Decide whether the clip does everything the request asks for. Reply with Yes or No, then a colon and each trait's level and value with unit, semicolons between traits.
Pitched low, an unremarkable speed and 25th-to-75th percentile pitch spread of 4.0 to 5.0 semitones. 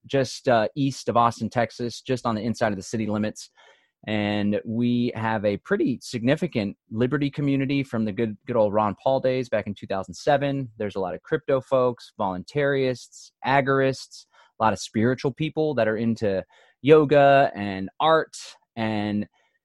Yes: low, 120 Hz; average, 160 wpm; average, 4.4 semitones